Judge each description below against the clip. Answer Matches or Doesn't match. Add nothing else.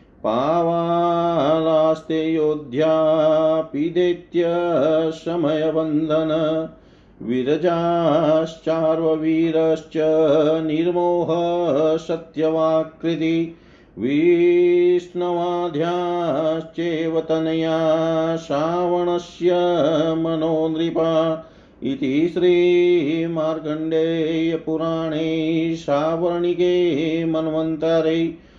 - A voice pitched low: Doesn't match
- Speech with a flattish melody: Matches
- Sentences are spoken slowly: Matches